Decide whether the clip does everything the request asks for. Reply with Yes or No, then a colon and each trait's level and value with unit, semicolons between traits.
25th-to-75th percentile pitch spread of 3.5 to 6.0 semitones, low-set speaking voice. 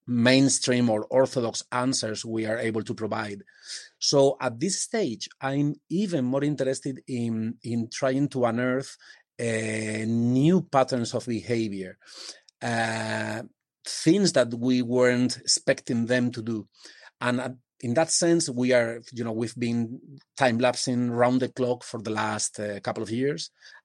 No: average, 2.7 semitones; low, 125 Hz